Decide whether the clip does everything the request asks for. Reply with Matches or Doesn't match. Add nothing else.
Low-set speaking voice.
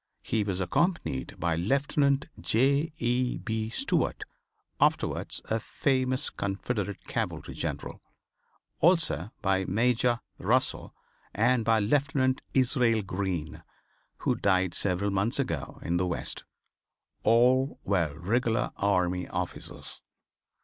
Matches